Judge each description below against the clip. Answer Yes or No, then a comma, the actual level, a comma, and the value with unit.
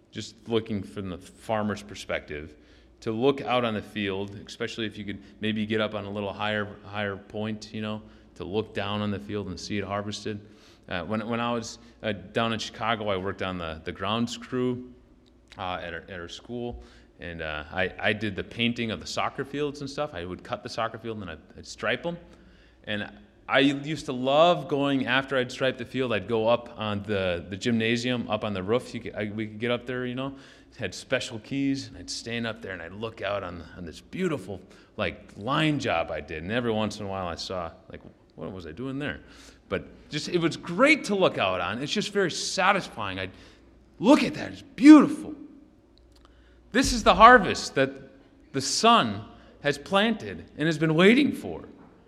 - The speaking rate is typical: No, fast, 215 wpm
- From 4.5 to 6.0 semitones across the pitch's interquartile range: Yes, average, 4.9 semitones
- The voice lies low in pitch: Yes, low, 110 Hz